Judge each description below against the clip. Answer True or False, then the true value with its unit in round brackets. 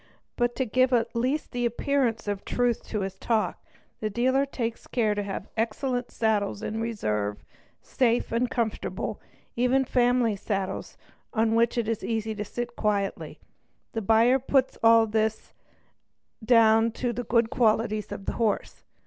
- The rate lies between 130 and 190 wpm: True (155 wpm)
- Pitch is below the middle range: False (230 Hz)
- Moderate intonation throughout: False (2.2 semitones)